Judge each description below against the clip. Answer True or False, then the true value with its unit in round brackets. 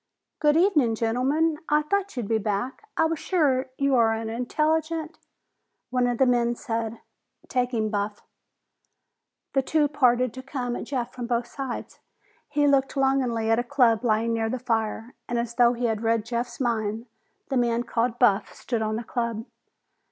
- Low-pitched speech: False (245 Hz)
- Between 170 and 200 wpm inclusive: True (180 wpm)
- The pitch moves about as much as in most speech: True (3.1 semitones)